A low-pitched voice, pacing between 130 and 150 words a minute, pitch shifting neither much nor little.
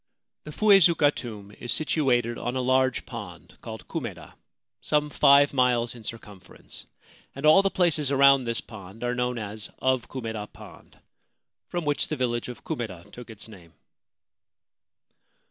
Yes: low, 125 Hz; average, 145 wpm; average, 4.2 semitones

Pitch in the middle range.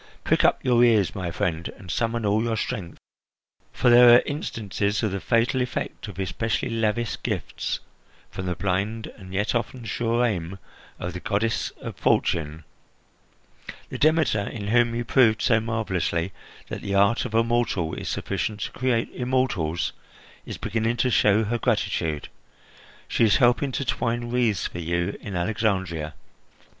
No: low, 110 Hz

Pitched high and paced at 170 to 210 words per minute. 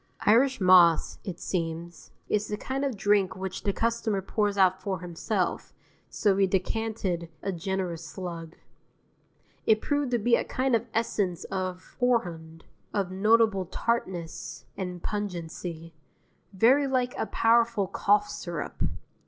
No: high, 195 Hz; slow, 135 wpm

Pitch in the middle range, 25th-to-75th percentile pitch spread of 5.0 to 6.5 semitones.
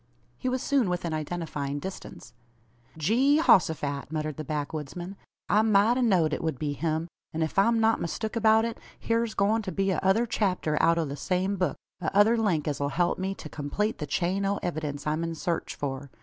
Yes: medium, 175 Hz; wide, 5.6 semitones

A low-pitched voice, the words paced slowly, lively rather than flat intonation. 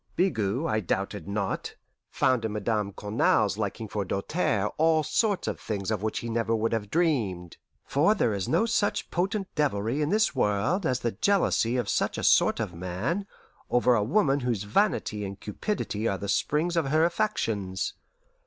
No: low, 115 Hz; average, 175 wpm; wide, 7.9 semitones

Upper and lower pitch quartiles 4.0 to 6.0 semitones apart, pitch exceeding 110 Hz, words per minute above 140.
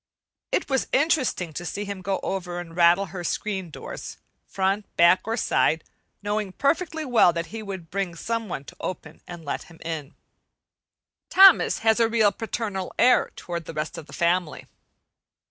Yes: average, 4.6 semitones; high, 190 Hz; average, 170 wpm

